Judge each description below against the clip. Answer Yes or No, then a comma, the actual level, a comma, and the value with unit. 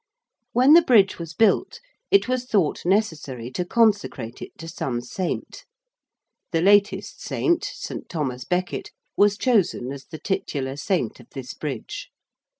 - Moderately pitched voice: Yes, medium, 180 Hz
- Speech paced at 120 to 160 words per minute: Yes, average, 145 wpm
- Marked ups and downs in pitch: Yes, wide, 7.8 semitones